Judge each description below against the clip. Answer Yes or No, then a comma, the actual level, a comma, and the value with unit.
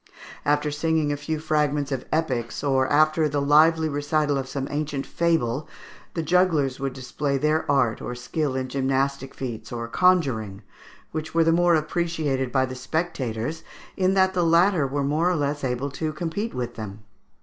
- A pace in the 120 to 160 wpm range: No, average, 170 wpm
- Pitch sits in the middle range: Yes, medium, 145 Hz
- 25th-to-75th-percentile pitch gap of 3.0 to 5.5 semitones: Yes, average, 3.3 semitones